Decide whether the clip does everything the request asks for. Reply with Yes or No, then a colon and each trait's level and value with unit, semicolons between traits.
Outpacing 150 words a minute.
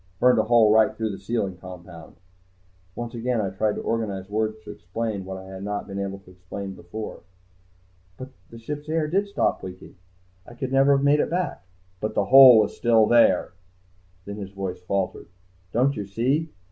Yes: average, 195 wpm